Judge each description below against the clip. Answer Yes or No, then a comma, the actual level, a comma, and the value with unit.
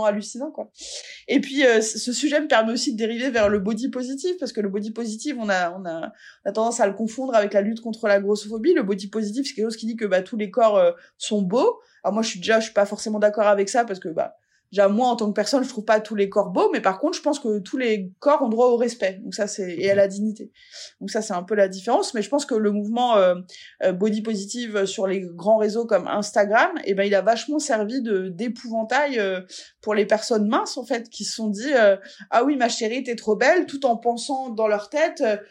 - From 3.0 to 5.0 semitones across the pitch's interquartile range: Yes, average, 4.2 semitones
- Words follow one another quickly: Yes, fast, 265 wpm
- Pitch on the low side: No, high, 225 Hz